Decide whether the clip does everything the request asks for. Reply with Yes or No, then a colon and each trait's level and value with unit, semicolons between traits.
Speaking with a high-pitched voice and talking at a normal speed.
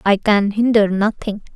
Yes: high, 205 Hz; average, 155 wpm